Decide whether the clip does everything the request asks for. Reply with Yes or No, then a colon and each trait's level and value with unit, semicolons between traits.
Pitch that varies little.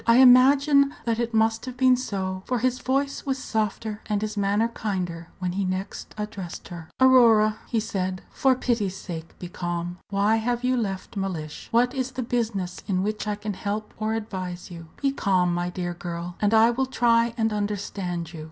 No: average, 4.4 semitones